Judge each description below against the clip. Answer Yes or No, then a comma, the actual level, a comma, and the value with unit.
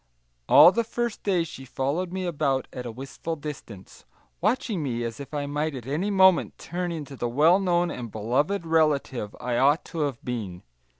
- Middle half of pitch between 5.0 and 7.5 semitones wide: Yes, wide, 5.6 semitones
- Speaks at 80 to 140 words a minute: No, average, 185 wpm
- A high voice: No, medium, 150 Hz